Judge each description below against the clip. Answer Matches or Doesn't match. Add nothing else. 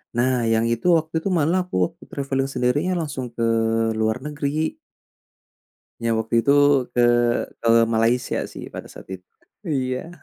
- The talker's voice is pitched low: Matches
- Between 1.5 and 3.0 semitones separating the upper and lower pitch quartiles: Doesn't match